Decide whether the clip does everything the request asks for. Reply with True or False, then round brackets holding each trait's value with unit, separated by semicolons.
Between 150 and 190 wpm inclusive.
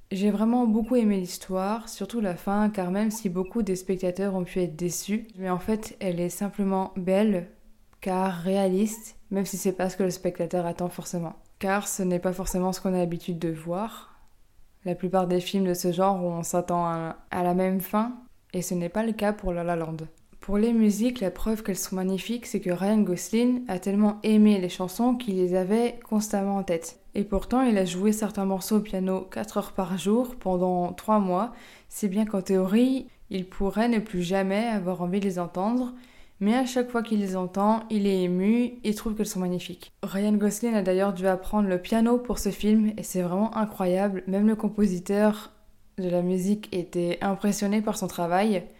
False (205 wpm)